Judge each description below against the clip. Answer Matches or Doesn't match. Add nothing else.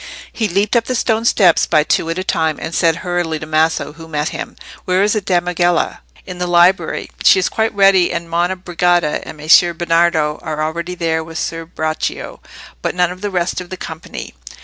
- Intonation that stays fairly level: Matches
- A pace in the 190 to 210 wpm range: Matches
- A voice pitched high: Doesn't match